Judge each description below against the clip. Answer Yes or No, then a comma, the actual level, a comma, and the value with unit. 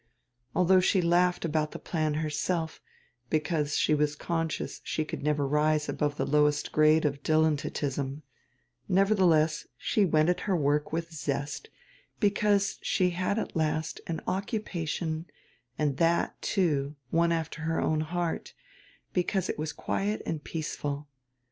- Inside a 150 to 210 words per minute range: No, average, 140 wpm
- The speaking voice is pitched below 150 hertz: No, medium, 160 Hz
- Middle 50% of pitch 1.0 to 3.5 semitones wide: Yes, average, 2.9 semitones